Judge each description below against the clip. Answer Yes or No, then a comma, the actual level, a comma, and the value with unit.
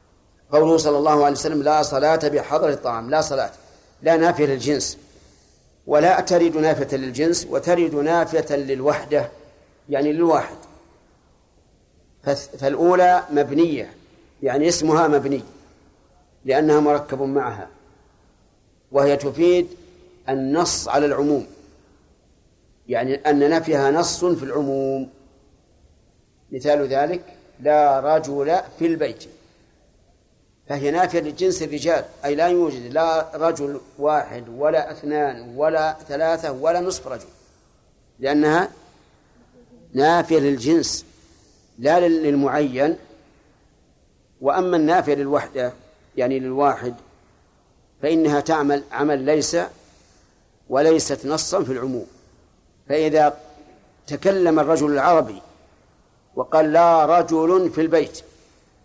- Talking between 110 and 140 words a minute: No, average, 95 wpm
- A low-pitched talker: No, medium, 145 Hz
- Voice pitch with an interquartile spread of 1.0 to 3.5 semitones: Yes, average, 2.8 semitones